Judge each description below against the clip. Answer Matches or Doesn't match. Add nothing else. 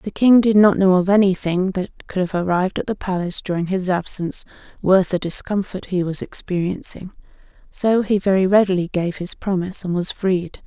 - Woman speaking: Matches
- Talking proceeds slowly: Doesn't match